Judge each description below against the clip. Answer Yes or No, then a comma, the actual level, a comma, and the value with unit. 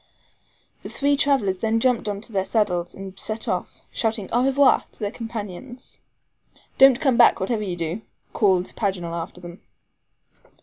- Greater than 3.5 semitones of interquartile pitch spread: Yes, average, 4.5 semitones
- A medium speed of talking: Yes, average, 150 wpm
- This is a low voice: No, high, 210 Hz